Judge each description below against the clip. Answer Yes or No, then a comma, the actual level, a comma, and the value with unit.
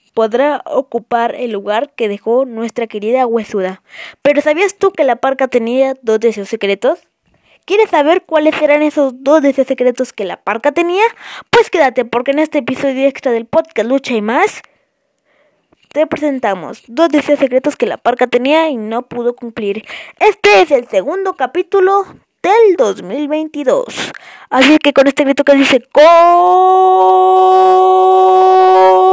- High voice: Yes, very high, 280 Hz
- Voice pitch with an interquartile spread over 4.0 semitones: Yes, wide, 5.4 semitones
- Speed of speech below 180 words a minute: Yes, average, 150 wpm